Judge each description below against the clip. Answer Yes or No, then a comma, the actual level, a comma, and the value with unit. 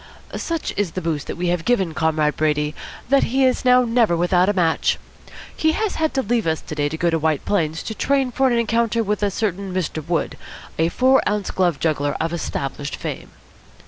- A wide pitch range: Yes, wide, 6.6 semitones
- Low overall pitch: No, medium, 185 Hz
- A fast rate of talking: Yes, fast, 210 wpm